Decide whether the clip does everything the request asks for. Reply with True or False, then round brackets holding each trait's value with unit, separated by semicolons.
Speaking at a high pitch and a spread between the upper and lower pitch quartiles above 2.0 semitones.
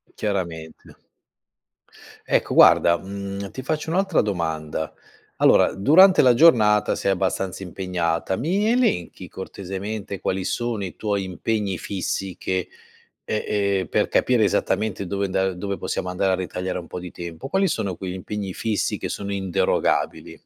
False (95 Hz; 2.7 semitones)